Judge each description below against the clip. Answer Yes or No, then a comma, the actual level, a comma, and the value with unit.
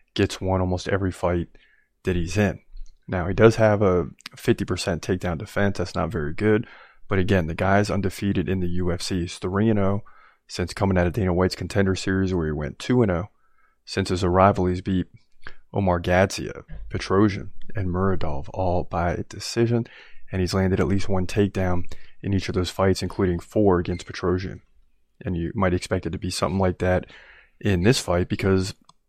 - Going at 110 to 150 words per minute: No, average, 175 wpm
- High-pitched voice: No, very low, 95 Hz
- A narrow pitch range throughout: Yes, narrow, 2.0 semitones